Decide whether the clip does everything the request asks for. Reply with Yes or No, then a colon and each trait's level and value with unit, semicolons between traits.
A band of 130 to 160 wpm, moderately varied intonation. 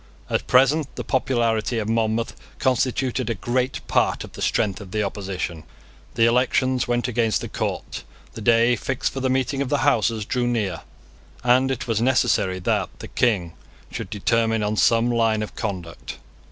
No: average, 170 wpm; average, 3.0 semitones